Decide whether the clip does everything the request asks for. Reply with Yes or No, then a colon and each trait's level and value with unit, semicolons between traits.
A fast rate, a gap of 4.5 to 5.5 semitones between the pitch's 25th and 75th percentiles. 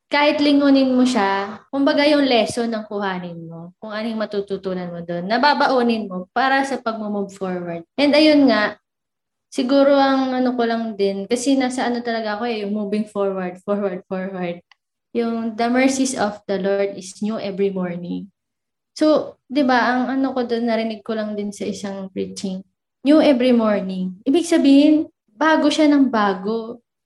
Yes: fast, 160 wpm; average, 5.1 semitones